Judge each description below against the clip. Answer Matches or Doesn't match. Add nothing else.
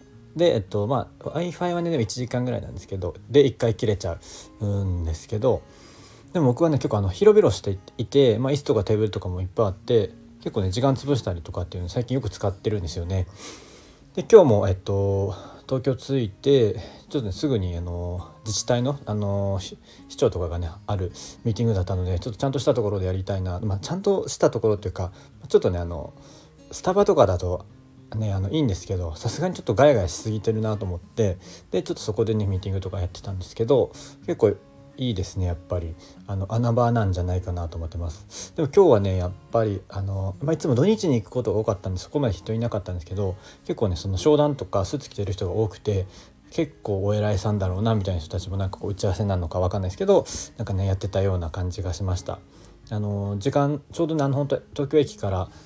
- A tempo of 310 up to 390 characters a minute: Doesn't match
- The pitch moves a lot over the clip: Doesn't match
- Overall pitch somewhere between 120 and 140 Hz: Doesn't match